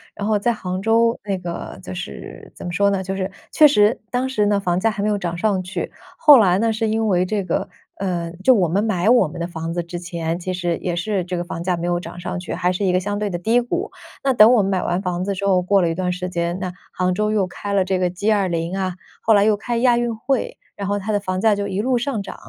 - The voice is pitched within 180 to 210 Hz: Yes, high, 190 Hz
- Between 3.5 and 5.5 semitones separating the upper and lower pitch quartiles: No, average, 3.1 semitones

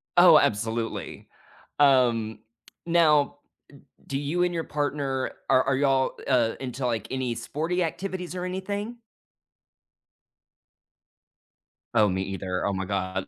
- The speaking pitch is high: No, low, 135 Hz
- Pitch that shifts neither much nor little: No, wide, 6.5 semitones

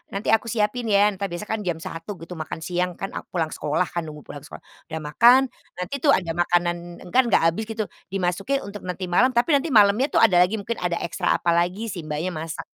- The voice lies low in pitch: No, medium, 180 Hz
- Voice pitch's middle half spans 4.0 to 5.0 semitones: Yes, average, 4.3 semitones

